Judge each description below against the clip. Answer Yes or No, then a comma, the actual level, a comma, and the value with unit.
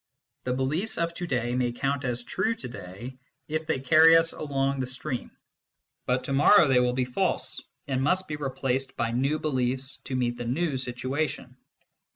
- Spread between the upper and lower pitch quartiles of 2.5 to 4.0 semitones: Yes, average, 3.5 semitones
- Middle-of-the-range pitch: No, low, 130 Hz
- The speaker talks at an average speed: Yes, average, 185 wpm